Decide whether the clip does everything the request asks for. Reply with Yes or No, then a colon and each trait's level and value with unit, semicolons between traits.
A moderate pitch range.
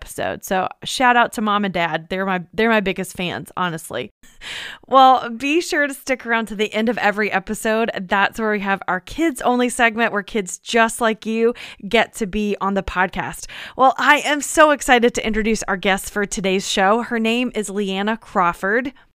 Yes: average, 3.6 semitones